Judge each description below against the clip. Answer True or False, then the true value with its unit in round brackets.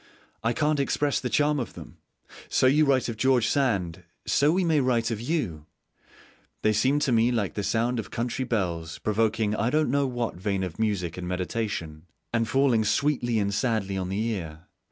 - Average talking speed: True (190 wpm)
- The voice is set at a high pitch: False (115 Hz)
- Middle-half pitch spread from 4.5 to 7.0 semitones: True (5.0 semitones)